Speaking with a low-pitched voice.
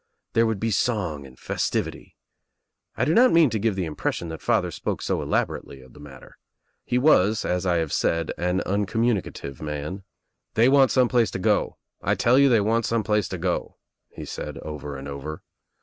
Yes: very low, 95 Hz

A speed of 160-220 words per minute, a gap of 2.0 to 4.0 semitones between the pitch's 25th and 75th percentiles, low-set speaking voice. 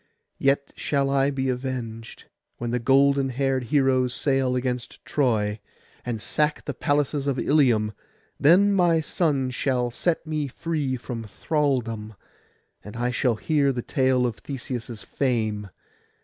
No: slow, 135 wpm; average, 2.8 semitones; low, 130 Hz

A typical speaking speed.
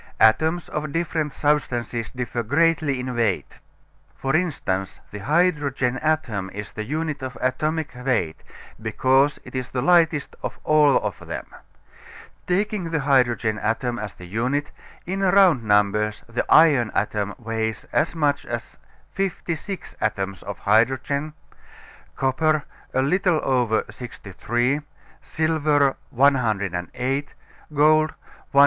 No: slow, 120 wpm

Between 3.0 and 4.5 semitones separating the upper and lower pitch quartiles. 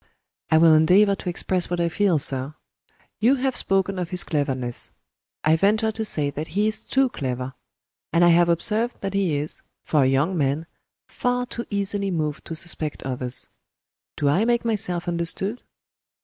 No: average, 5.2 semitones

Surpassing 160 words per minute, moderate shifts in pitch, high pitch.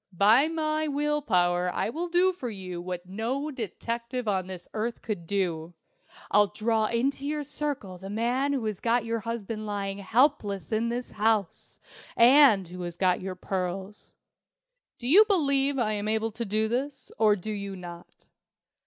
No: average, 170 wpm; wide, 5.7 semitones; high, 220 Hz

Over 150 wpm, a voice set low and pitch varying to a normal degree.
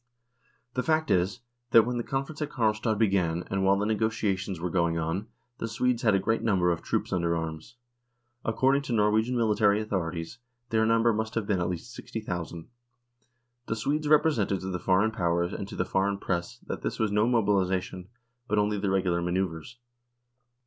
Yes: average, 185 wpm; low, 105 Hz; average, 4.0 semitones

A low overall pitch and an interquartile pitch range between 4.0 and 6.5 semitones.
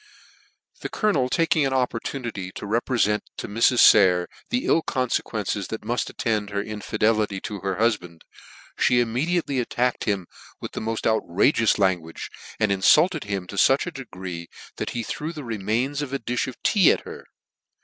Yes: low, 115 Hz; average, 4.6 semitones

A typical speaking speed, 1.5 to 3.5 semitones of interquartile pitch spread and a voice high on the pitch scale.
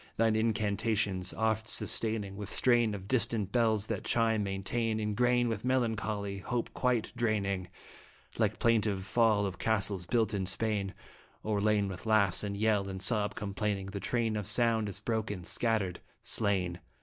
No: average, 150 wpm; narrow, 2.4 semitones; low, 105 Hz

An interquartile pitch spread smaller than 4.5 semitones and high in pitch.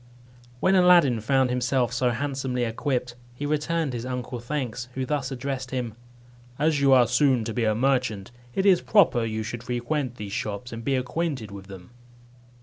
No: average, 2.9 semitones; low, 125 Hz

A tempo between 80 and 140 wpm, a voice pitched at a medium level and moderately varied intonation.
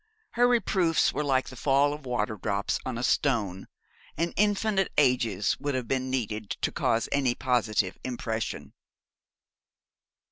No: slow, 135 wpm; low, 130 Hz; average, 4.6 semitones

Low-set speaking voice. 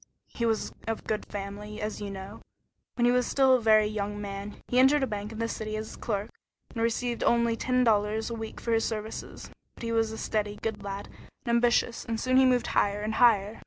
No: high, 220 Hz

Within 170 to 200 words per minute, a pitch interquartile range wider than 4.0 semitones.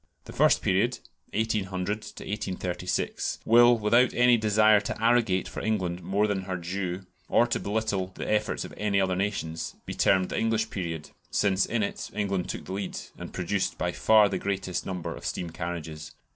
No: average, 175 wpm; average, 2.9 semitones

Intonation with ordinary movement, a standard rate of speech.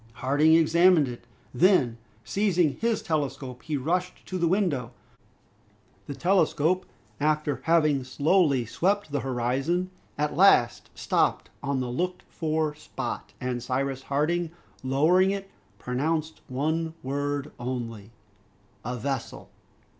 No: average, 4.9 semitones; slow, 115 wpm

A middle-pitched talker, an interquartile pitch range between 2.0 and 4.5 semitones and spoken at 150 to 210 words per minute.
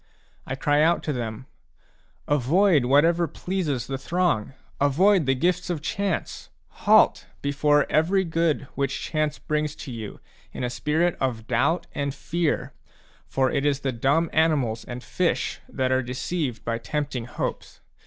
Yes: medium, 145 Hz; average, 4.2 semitones; average, 155 wpm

